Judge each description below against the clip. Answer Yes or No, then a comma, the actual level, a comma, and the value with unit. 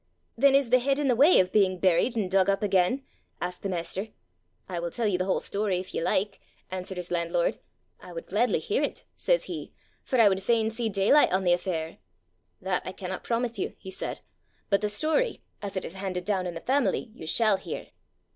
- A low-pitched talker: No, high, 195 Hz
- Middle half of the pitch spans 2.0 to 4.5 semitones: Yes, average, 4.2 semitones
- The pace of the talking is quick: Yes, fast, 220 wpm